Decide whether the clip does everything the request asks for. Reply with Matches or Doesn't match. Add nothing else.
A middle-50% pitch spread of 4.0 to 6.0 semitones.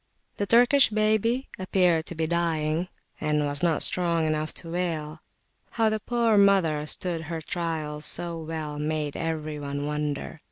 Doesn't match